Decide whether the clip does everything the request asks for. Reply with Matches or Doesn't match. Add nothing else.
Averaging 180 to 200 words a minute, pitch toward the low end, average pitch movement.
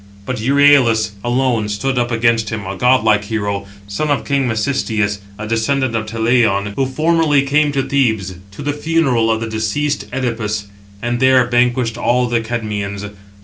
Doesn't match